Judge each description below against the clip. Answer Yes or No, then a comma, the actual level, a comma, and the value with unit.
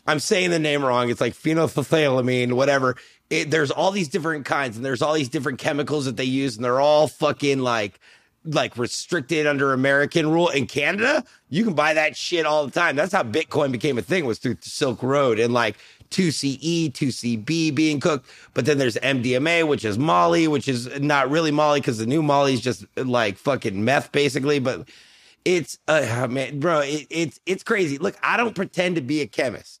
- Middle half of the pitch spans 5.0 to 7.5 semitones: No, average, 3.2 semitones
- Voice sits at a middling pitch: Yes, medium, 145 Hz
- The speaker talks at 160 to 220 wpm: Yes, average, 200 wpm